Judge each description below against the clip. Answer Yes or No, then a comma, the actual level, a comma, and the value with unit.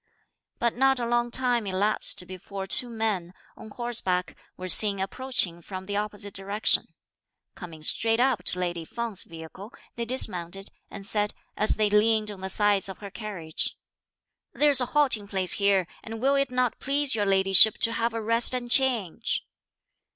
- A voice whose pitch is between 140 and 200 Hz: No, high, 210 Hz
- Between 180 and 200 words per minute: No, average, 165 wpm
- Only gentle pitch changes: No, average, 3.8 semitones